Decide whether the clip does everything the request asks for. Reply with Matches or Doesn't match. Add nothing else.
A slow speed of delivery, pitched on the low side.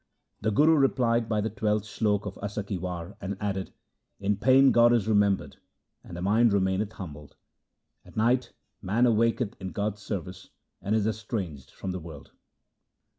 Doesn't match